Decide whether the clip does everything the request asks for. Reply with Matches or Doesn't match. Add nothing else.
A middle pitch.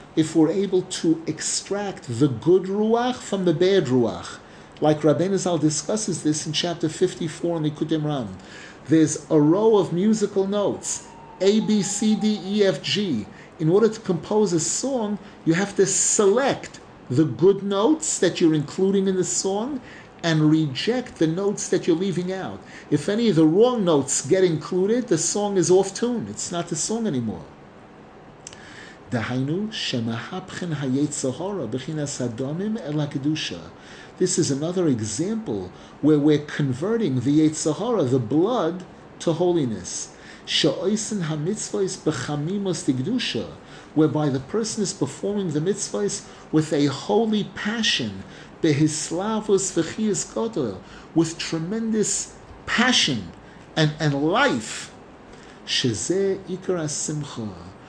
Matches